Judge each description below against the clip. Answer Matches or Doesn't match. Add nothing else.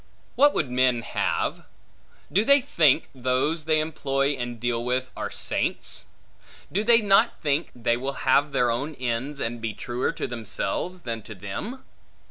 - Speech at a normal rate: Matches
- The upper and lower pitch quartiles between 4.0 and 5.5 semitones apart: Matches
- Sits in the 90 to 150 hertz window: Matches